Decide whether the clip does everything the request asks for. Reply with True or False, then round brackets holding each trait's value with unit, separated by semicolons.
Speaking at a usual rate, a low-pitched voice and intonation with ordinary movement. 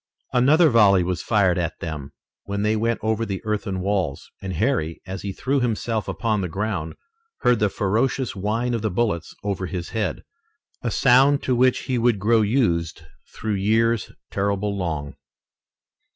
True (165 wpm; 105 Hz; 3.7 semitones)